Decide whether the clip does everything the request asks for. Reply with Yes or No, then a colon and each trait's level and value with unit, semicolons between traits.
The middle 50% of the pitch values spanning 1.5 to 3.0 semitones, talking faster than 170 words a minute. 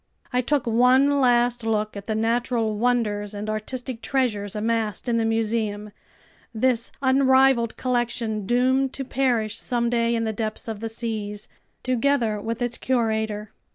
No: narrow, 2.5 semitones; average, 145 wpm